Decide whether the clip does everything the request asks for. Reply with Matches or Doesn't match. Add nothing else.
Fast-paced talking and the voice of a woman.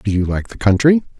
Doesn't match